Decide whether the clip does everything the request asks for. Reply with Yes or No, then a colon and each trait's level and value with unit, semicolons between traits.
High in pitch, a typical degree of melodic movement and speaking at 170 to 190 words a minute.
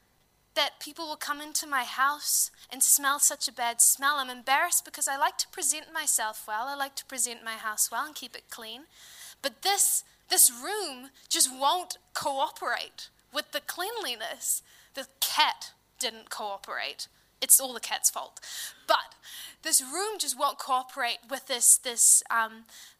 No: very high, 275 Hz; average, 4.0 semitones; average, 160 wpm